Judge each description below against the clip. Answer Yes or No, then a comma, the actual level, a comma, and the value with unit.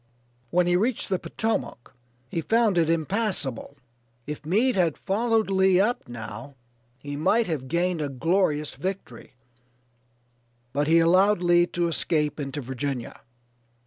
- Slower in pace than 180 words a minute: Yes, slow, 135 wpm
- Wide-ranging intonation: No, average, 5.0 semitones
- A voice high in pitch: No, medium, 170 Hz